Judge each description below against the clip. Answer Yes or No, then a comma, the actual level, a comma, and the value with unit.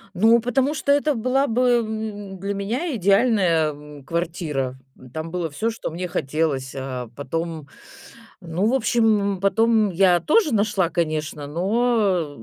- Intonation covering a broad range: Yes, wide, 5.8 semitones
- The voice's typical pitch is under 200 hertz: Yes, high, 190 Hz